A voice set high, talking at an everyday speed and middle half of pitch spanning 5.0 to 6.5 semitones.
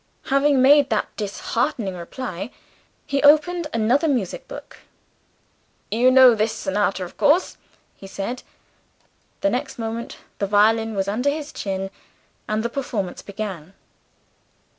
No: high, 225 Hz; slow, 125 wpm; wide, 5.4 semitones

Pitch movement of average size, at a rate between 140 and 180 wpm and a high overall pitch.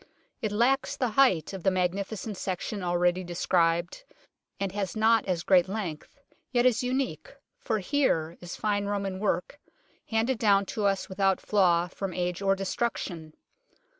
Yes: average, 3.6 semitones; average, 150 wpm; high, 195 Hz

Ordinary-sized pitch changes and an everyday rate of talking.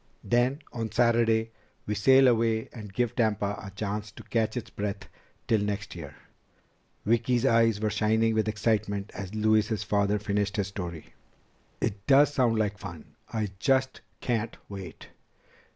No: narrow, 2.2 semitones; average, 150 wpm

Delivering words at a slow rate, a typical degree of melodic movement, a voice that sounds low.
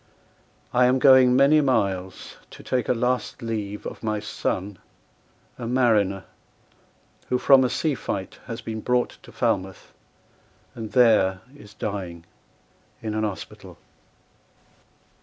Yes: slow, 125 wpm; average, 4.0 semitones; low, 110 Hz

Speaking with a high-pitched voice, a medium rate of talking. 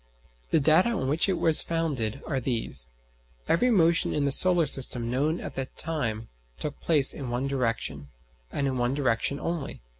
No: medium, 140 Hz; average, 175 wpm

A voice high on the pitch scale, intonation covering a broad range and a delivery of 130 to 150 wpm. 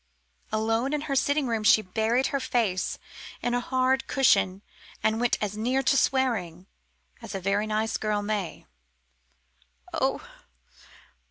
No: high, 225 Hz; average, 3.7 semitones; average, 140 wpm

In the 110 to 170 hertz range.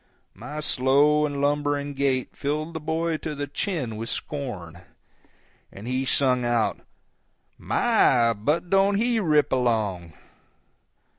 Yes: medium, 140 Hz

